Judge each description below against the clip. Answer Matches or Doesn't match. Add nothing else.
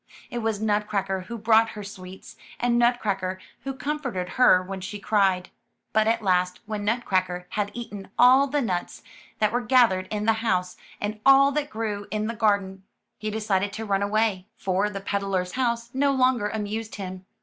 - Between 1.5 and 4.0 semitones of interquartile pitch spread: Matches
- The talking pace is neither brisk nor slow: Matches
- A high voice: Matches